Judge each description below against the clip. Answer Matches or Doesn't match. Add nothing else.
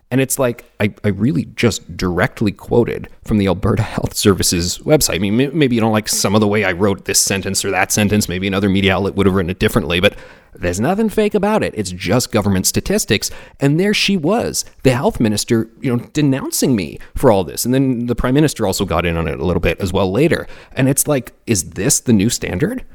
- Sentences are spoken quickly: Matches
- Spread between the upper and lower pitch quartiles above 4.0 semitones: Matches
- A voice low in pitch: Matches